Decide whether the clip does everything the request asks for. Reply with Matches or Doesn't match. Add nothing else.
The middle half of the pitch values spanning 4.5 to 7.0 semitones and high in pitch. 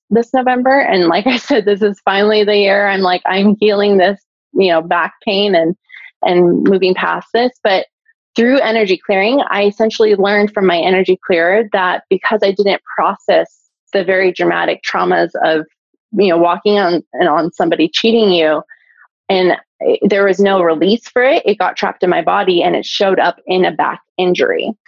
Doesn't match